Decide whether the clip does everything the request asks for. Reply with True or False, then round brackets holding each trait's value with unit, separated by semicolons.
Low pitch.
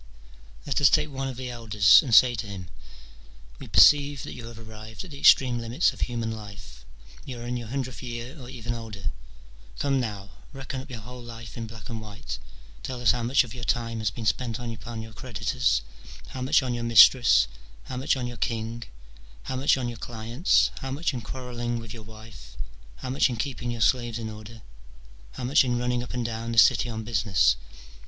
True (115 Hz)